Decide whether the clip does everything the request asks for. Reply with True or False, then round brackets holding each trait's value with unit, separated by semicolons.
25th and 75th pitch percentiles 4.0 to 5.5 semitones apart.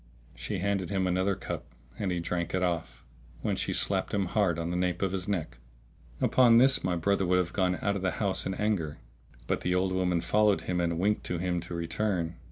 False (2.5 semitones)